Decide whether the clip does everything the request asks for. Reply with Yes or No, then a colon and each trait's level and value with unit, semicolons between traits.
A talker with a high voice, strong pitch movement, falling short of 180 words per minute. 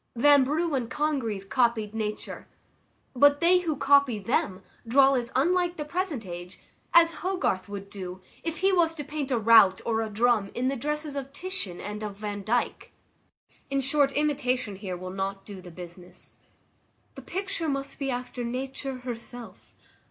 Yes: very high, 250 Hz; wide, 6.0 semitones; average, 160 wpm